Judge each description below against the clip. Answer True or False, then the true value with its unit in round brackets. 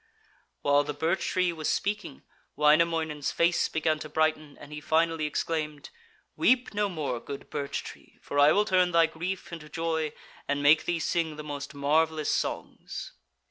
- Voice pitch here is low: False (155 Hz)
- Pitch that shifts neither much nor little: False (2.1 semitones)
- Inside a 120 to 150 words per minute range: False (165 wpm)